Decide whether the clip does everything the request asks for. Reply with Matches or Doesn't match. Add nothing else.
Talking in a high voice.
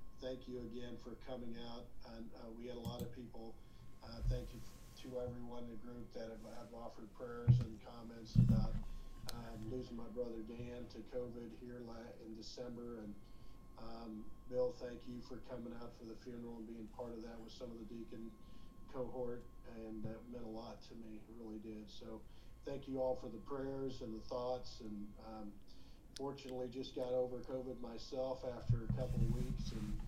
Doesn't match